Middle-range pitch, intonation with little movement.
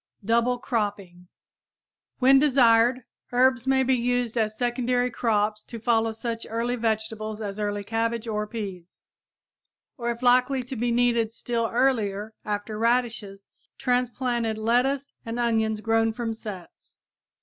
No: high, 230 Hz; narrow, 2.2 semitones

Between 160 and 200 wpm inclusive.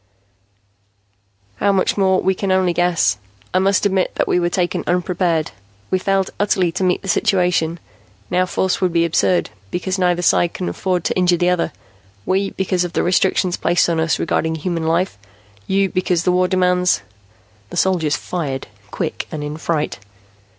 Yes: average, 175 wpm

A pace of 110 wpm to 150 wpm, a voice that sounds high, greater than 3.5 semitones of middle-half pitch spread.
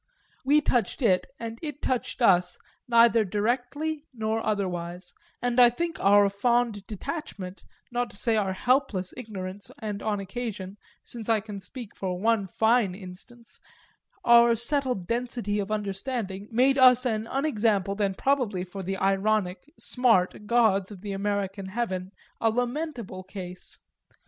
Yes: average, 140 wpm; high, 215 Hz; average, 3.9 semitones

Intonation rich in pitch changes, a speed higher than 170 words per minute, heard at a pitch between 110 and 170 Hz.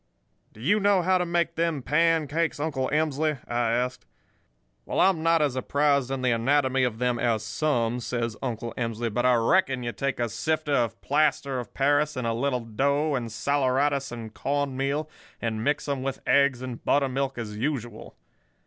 No: average, 3.8 semitones; average, 180 wpm; low, 135 Hz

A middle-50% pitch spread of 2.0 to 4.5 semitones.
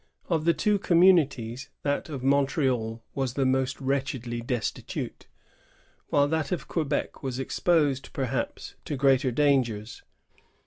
Yes: average, 2.7 semitones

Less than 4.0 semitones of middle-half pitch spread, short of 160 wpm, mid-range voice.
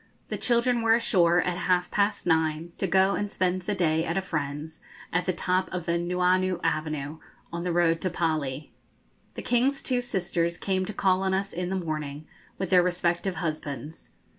No: average, 2.7 semitones; average, 190 wpm; medium, 180 Hz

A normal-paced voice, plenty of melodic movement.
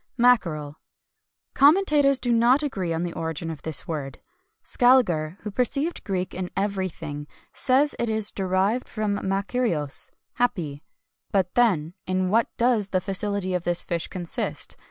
Yes: average, 150 wpm; wide, 6.1 semitones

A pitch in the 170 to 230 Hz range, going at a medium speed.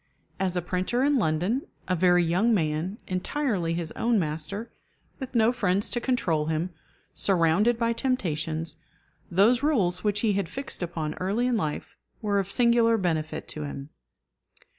Yes: high, 190 Hz; average, 155 wpm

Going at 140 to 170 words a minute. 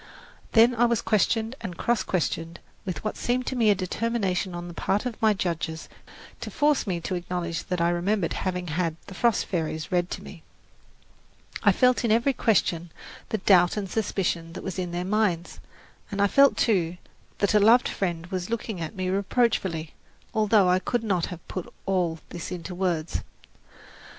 No: average, 180 wpm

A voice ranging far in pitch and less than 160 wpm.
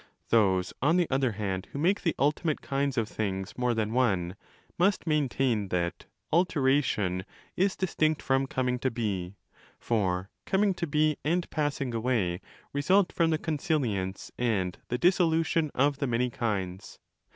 Yes: wide, 7.0 semitones; average, 150 wpm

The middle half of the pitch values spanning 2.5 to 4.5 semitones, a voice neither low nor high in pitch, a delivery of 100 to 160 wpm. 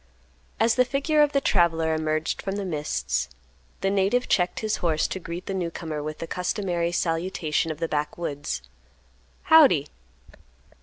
Yes: average, 4.1 semitones; medium, 175 Hz; average, 150 wpm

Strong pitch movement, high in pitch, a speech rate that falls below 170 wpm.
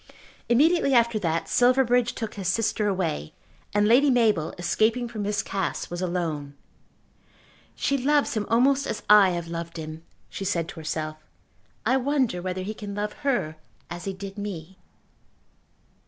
Yes: wide, 5.7 semitones; high, 205 Hz; average, 155 wpm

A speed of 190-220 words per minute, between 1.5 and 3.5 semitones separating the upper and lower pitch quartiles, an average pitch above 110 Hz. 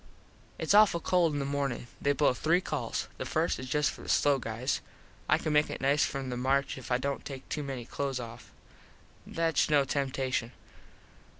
Yes: average, 195 wpm; narrow, 2.4 semitones; medium, 140 Hz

